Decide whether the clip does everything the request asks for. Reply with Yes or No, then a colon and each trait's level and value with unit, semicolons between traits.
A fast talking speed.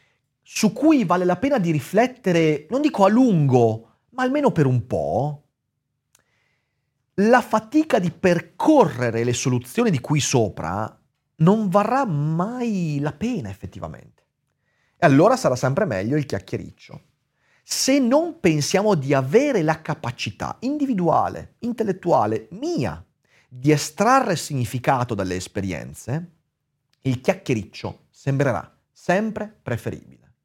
No: slow, 115 wpm